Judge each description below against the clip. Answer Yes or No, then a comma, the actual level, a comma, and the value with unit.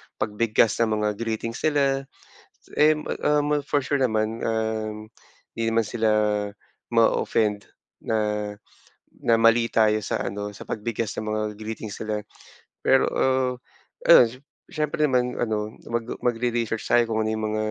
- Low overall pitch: Yes, low, 115 Hz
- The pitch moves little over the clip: Yes, narrow, 2.3 semitones